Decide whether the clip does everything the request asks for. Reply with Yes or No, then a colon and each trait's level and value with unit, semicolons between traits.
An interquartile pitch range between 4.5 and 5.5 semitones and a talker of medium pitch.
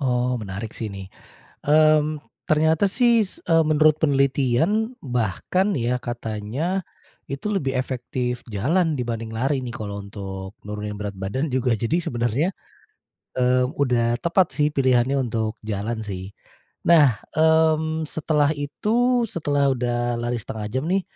No: average, 5.2 semitones; low, 130 Hz